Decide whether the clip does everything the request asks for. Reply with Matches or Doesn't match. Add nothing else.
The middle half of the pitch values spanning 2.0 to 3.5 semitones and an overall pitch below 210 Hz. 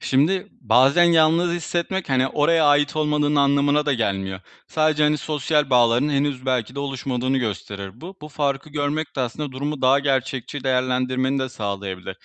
Matches